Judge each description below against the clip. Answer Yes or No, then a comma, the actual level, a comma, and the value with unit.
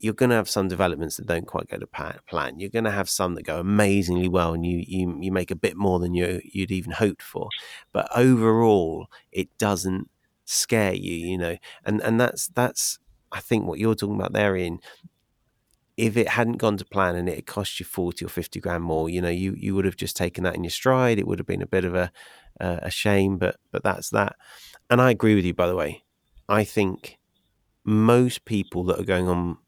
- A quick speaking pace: Yes, fast, 225 wpm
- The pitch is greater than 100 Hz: No, very low, 95 Hz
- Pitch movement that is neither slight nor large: Yes, average, 3.2 semitones